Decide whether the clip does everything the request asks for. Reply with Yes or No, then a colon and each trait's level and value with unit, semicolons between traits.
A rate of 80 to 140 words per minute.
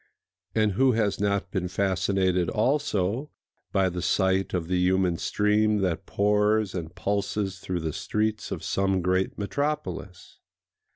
Yes: slow, 135 wpm